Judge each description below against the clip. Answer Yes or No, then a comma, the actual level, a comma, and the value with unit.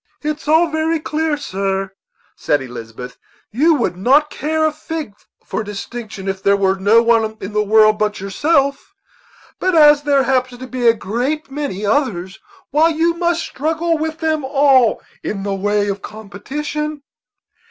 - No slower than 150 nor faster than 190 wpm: Yes, average, 160 wpm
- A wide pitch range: Yes, wide, 7.1 semitones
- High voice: Yes, very high, 255 Hz